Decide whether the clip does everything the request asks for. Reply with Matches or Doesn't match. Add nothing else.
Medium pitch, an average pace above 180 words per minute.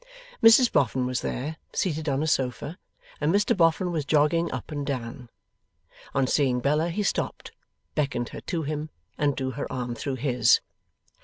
Doesn't match